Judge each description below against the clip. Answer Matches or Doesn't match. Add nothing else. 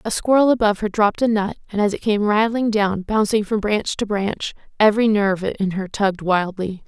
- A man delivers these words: Doesn't match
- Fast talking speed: Matches